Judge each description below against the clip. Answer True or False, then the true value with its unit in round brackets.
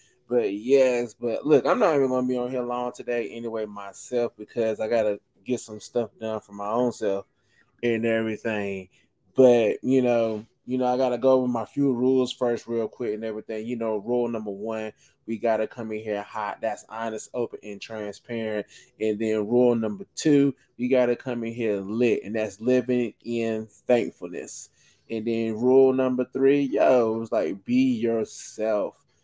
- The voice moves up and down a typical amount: False (2.3 semitones)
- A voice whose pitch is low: True (115 Hz)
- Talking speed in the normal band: True (180 wpm)